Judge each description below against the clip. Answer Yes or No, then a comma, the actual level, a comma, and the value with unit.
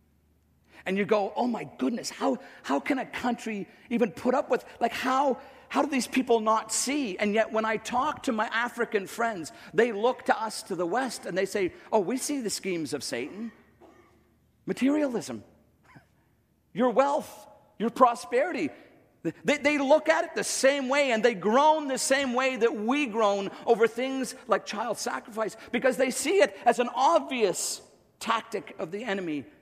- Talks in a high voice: Yes, high, 235 Hz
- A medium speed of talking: Yes, average, 175 wpm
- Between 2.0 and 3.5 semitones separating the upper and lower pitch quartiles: No, average, 4.2 semitones